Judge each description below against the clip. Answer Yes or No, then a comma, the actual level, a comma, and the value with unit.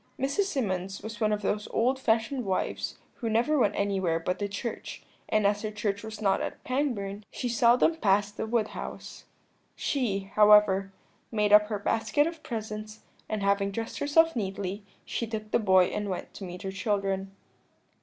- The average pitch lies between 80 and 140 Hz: No, high, 210 Hz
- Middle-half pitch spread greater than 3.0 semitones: No, narrow, 2.6 semitones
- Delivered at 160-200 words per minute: Yes, average, 175 wpm